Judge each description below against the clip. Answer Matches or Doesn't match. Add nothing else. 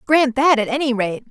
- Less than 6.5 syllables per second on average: Matches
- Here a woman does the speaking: Matches